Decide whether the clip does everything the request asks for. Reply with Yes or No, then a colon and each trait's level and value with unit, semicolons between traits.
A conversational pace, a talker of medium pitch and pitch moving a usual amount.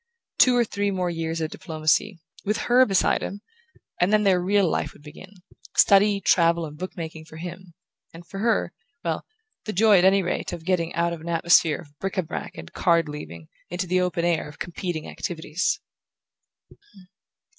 Yes: average, 185 wpm; medium, 175 Hz; average, 3.0 semitones